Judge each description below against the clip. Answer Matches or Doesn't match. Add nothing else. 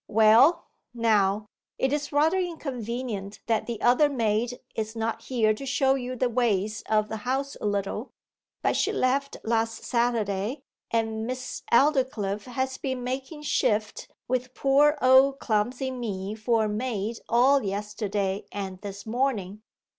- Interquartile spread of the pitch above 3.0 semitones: Matches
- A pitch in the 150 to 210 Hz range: Doesn't match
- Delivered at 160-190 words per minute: Doesn't match